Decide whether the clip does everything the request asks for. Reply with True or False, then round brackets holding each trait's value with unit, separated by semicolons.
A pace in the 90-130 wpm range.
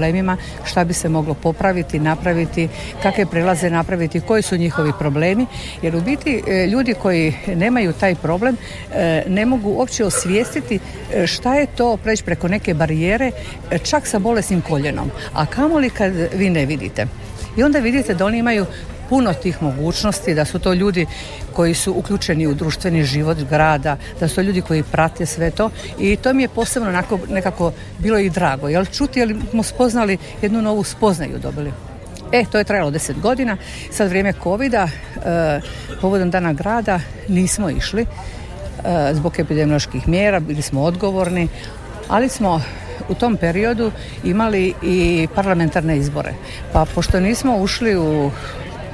False (155 wpm)